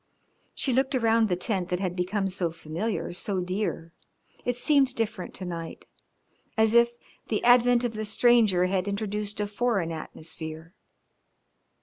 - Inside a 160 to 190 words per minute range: No, average, 145 wpm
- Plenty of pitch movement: No, average, 4.4 semitones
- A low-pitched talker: No, high, 205 Hz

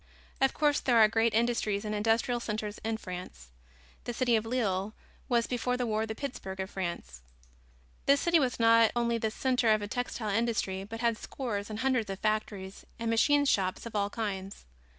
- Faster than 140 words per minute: Yes, average, 190 wpm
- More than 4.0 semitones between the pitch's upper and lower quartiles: No, average, 2.8 semitones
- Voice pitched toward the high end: Yes, high, 225 Hz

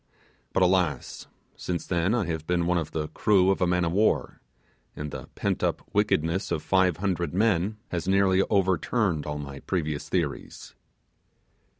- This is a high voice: No, very low, 90 Hz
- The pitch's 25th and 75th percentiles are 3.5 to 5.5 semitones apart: No, average, 2.9 semitones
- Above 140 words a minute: Yes, average, 165 wpm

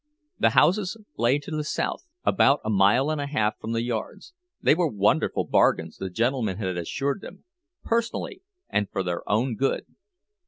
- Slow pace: No, average, 165 wpm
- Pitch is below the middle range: Yes, low, 130 Hz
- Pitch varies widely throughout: Yes, wide, 6.7 semitones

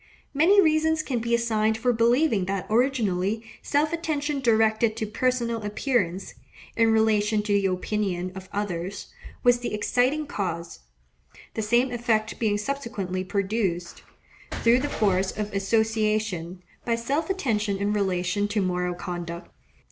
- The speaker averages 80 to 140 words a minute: Yes, slow, 135 wpm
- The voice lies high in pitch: Yes, high, 215 Hz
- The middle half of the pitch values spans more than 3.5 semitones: Yes, average, 3.9 semitones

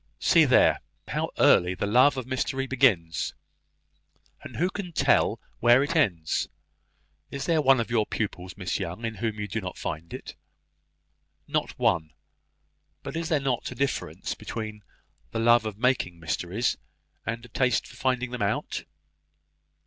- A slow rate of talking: No, average, 160 wpm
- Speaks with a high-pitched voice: No, low, 115 Hz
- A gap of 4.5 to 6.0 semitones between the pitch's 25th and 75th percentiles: Yes, average, 5.2 semitones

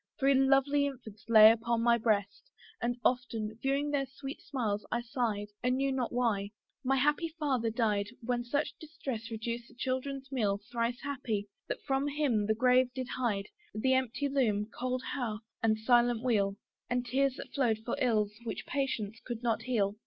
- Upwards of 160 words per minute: Yes, average, 175 wpm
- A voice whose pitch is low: No, high, 245 Hz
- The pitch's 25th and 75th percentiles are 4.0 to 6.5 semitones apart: No, average, 3.4 semitones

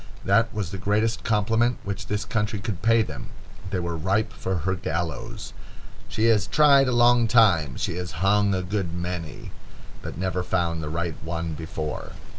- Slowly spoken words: No, average, 175 wpm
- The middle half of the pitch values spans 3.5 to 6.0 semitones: Yes, average, 4.5 semitones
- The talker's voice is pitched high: No, very low, 95 Hz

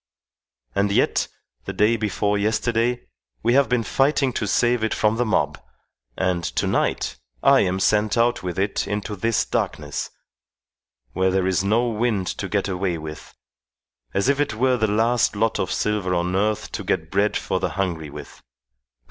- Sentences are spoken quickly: No, average, 175 wpm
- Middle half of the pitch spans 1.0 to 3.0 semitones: No, average, 3.7 semitones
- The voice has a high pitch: No, low, 105 Hz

